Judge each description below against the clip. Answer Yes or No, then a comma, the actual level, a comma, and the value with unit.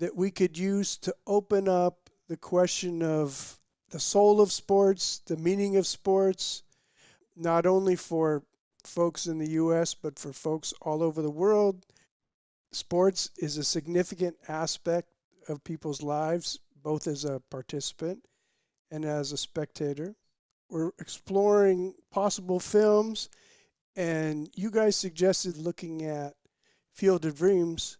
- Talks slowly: Yes, slow, 130 wpm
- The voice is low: No, medium, 175 Hz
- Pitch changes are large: No, average, 3.5 semitones